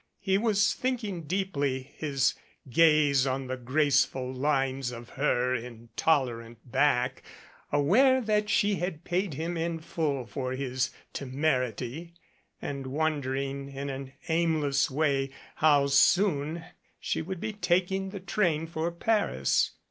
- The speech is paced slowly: Yes, slow, 125 wpm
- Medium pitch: Yes, medium, 145 Hz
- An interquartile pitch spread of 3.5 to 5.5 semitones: Yes, average, 4.6 semitones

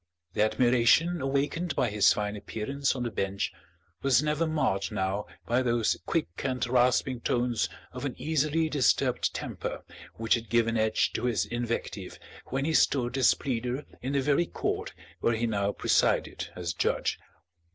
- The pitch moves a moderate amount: Yes, average, 4.1 semitones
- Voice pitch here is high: No, low, 120 Hz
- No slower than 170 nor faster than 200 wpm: No, average, 160 wpm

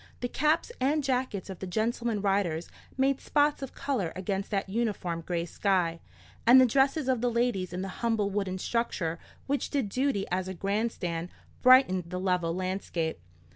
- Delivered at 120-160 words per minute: No, average, 175 wpm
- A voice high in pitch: Yes, high, 200 Hz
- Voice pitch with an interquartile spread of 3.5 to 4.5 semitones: No, wide, 5.6 semitones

